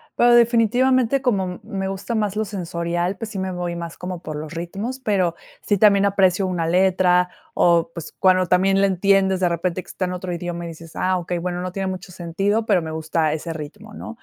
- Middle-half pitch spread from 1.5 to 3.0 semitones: Yes, narrow, 2.6 semitones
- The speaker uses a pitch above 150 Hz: Yes, medium, 185 Hz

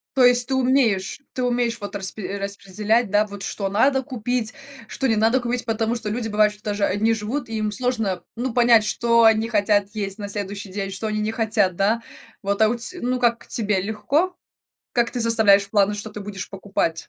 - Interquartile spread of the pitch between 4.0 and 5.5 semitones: No, average, 2.8 semitones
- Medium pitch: No, high, 220 Hz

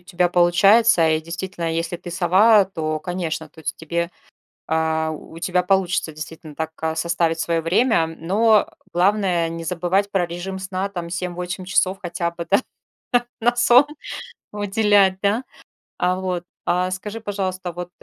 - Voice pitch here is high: No, medium, 180 Hz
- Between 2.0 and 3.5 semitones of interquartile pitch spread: Yes, narrow, 2.6 semitones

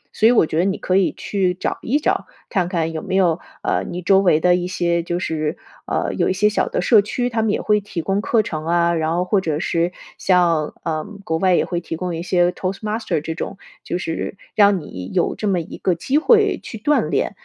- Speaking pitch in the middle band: Yes, medium, 180 Hz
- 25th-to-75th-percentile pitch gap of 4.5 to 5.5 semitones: No, average, 3.3 semitones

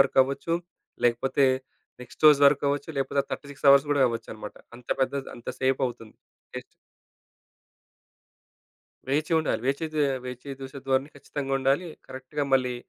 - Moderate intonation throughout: No, narrow, 1.6 semitones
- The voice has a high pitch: No, low, 135 Hz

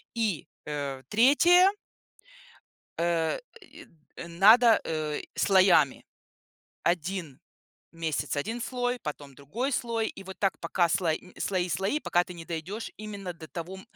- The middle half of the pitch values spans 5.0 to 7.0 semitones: Yes, wide, 5.6 semitones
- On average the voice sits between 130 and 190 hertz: Yes, medium, 185 Hz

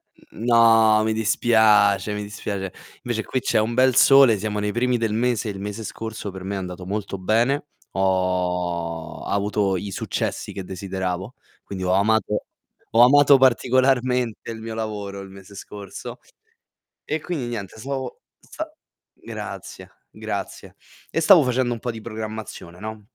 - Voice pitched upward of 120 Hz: No, low, 110 Hz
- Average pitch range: Yes, average, 3.5 semitones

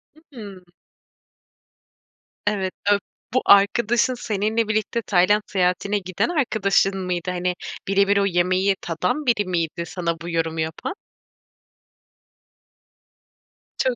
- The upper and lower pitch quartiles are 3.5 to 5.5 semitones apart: No, average, 3.0 semitones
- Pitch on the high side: Yes, high, 195 Hz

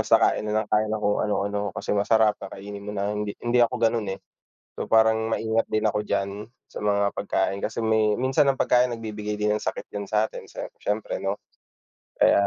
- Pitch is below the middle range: Yes, low, 105 Hz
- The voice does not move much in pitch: Yes, narrow, 1.5 semitones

